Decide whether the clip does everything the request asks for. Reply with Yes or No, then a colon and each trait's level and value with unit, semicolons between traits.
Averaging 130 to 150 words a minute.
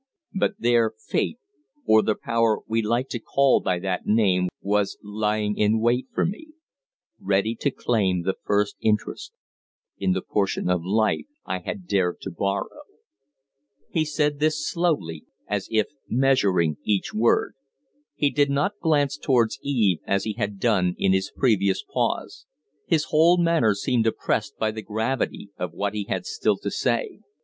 No: average, 160 wpm